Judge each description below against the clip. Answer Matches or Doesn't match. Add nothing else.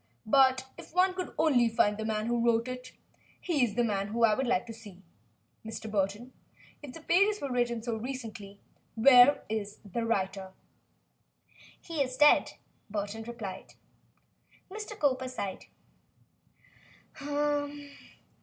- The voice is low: Doesn't match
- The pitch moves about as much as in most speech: Matches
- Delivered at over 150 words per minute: Doesn't match